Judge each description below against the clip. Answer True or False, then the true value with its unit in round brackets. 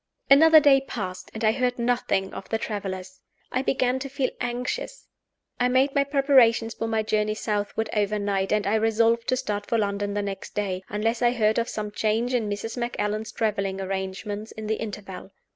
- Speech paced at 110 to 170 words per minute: False (185 wpm)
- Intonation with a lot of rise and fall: False (3.1 semitones)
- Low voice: False (220 Hz)